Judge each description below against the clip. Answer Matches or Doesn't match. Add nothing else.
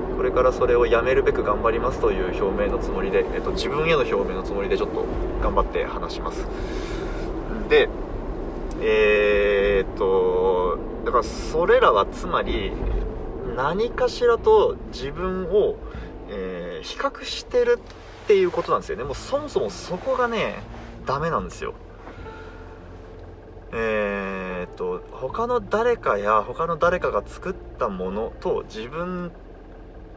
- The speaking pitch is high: Matches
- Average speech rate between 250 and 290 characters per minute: Matches